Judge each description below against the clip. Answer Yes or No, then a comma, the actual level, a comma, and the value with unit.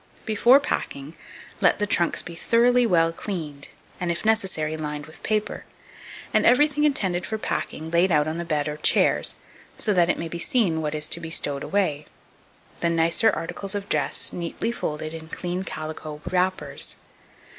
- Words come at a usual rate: Yes, average, 170 wpm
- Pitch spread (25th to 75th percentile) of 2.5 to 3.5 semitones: No, average, 4.6 semitones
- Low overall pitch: No, medium, 170 Hz